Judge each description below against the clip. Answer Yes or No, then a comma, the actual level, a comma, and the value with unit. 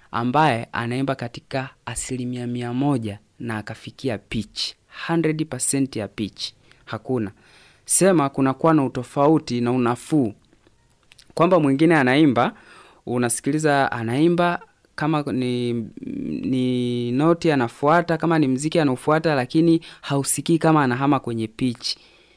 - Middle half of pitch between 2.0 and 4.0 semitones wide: No, average, 4.4 semitones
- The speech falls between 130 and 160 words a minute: No, average, 105 wpm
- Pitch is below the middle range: Yes, low, 130 Hz